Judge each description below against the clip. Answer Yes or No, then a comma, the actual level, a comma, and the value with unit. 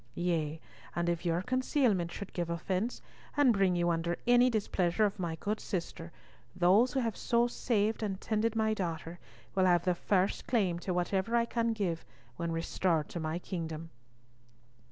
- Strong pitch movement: No, average, 4.3 semitones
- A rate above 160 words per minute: Yes, average, 170 wpm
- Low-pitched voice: No, medium, 185 Hz